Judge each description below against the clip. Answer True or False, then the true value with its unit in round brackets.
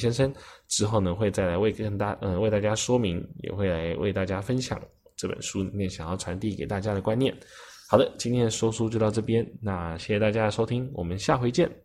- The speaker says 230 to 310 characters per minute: False (330 characters per minute)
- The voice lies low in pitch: True (105 Hz)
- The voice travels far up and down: False (2.9 semitones)